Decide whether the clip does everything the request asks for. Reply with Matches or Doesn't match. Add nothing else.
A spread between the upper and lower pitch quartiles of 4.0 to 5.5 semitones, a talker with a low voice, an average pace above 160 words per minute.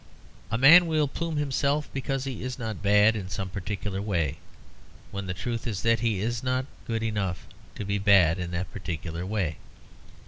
Matches